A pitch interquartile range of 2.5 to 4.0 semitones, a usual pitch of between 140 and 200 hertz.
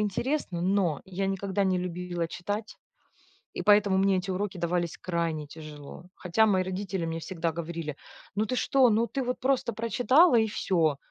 Yes: average, 3.7 semitones; high, 190 Hz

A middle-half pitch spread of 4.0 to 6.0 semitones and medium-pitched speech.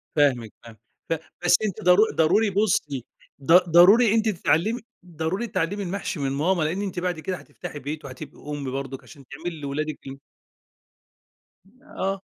Yes: average, 5.1 semitones; medium, 165 Hz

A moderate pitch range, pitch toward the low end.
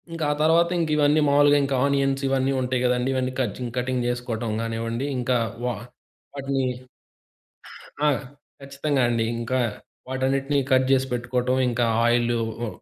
No: narrow, 2.1 semitones; low, 130 Hz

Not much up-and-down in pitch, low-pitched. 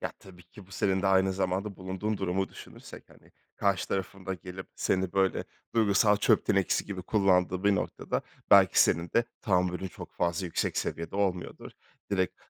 Yes: narrow, 1.4 semitones; very low, 95 Hz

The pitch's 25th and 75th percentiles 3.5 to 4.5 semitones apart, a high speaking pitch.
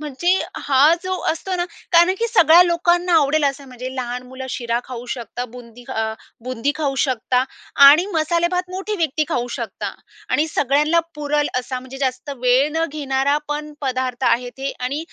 Yes: average, 4.1 semitones; very high, 280 Hz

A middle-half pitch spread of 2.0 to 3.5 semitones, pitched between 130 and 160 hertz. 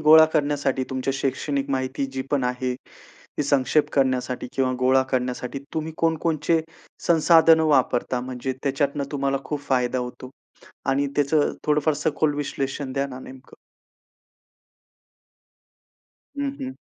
Yes: narrow, 2.5 semitones; medium, 140 Hz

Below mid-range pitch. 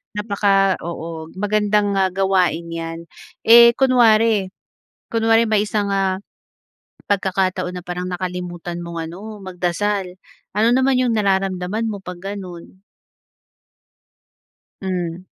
No: high, 190 Hz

